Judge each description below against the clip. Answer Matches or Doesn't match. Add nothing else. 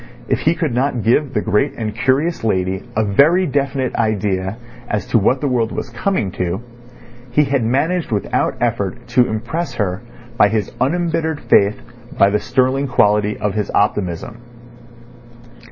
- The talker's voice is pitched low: Matches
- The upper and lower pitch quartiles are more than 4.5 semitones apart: Matches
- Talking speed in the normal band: Matches